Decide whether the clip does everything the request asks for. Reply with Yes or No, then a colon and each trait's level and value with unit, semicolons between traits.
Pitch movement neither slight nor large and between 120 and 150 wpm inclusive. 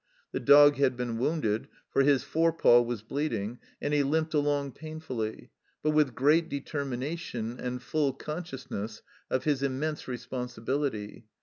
Yes: average, 3.8 semitones; average, 140 wpm